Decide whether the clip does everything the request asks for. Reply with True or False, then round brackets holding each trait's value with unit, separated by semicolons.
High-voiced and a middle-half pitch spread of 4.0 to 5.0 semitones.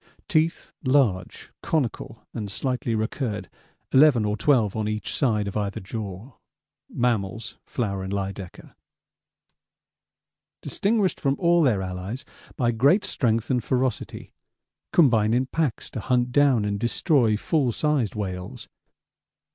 False (115 Hz; 4.6 semitones)